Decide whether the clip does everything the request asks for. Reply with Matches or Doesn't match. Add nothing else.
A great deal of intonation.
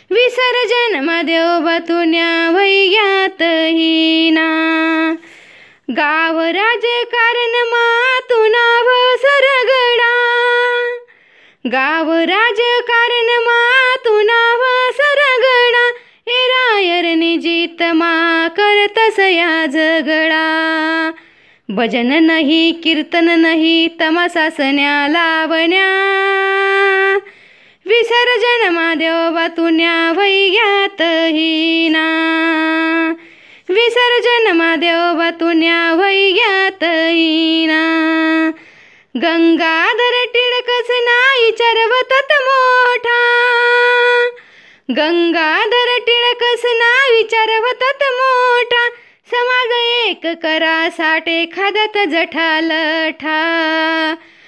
Matches